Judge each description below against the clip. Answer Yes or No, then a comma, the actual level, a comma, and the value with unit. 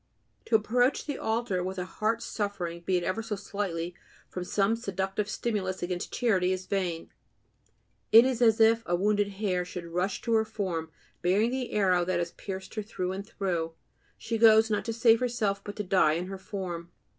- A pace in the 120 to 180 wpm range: No, average, 190 wpm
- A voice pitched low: No, high, 200 Hz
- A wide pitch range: No, average, 3.5 semitones